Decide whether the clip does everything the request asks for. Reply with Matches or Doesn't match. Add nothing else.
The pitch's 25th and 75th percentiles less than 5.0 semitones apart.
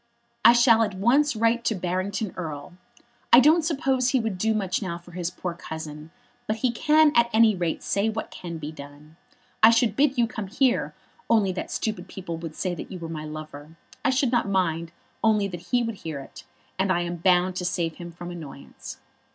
Doesn't match